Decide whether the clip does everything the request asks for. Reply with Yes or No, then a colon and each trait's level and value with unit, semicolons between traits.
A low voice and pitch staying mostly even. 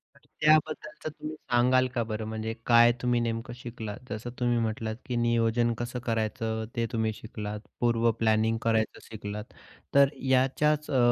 Yes: low, 115 Hz; narrow, 2.0 semitones